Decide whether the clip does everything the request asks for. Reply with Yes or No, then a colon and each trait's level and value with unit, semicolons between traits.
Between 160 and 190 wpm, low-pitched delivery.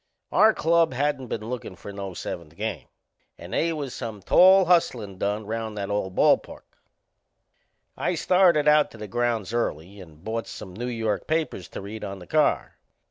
Yes: average, 180 wpm; low, 110 Hz